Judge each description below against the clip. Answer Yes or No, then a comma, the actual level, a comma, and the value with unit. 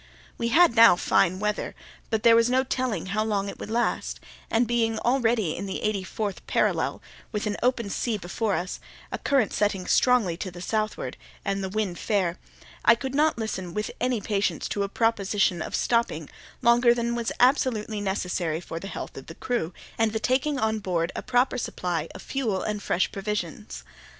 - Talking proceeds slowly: No, average, 190 wpm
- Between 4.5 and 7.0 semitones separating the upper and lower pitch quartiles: No, average, 3.8 semitones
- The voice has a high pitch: Yes, high, 215 Hz